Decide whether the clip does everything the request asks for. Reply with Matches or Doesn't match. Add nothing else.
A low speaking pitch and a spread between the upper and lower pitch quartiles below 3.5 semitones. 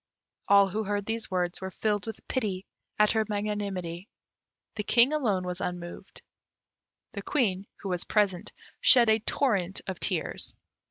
Doesn't match